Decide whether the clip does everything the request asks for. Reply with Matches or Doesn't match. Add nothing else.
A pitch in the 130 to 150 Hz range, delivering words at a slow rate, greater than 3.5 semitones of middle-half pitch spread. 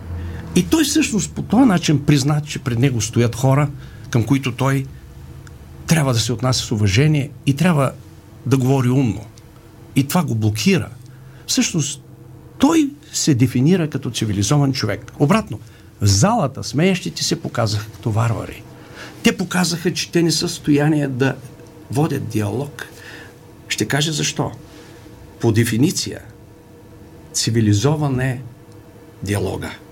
Doesn't match